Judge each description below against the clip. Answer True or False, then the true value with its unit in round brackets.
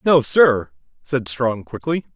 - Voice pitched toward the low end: True (125 Hz)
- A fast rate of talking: False (140 wpm)